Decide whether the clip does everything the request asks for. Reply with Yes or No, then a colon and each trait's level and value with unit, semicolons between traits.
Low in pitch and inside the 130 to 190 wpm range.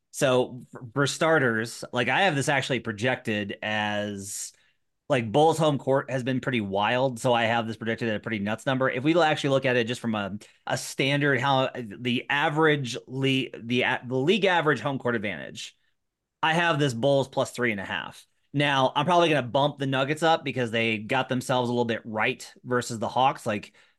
No: low, 125 Hz; average, 200 wpm